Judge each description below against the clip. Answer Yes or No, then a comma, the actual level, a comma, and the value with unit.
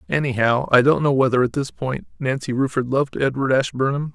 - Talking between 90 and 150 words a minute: No, average, 190 wpm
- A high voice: No, low, 135 Hz